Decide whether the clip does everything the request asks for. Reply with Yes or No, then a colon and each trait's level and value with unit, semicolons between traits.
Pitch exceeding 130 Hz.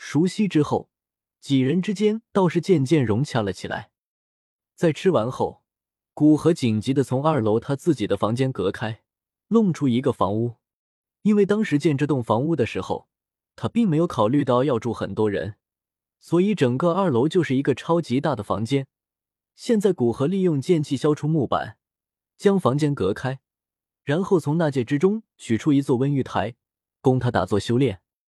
Yes: medium, 140 Hz